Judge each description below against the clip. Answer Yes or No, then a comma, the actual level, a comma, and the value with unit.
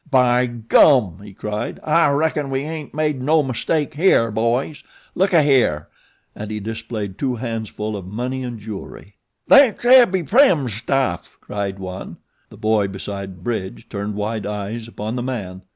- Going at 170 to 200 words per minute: No, average, 150 wpm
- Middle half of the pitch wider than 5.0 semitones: Yes, wide, 5.4 semitones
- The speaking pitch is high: No, low, 115 Hz